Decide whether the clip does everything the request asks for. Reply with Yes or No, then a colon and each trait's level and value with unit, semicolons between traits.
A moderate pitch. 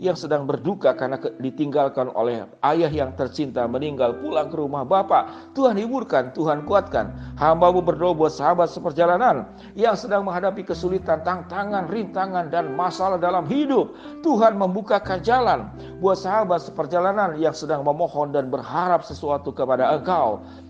Yes: medium, 175 Hz